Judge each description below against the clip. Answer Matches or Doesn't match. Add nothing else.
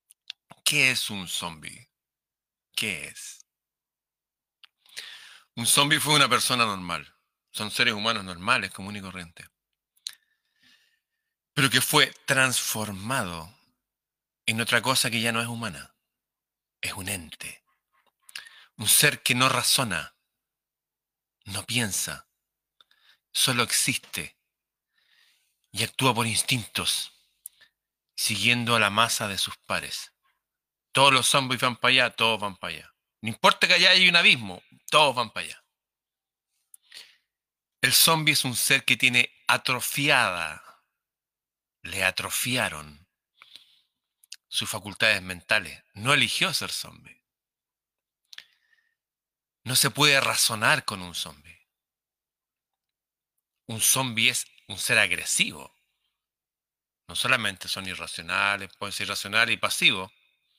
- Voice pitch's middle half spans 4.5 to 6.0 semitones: Matches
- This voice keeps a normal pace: Doesn't match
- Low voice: Matches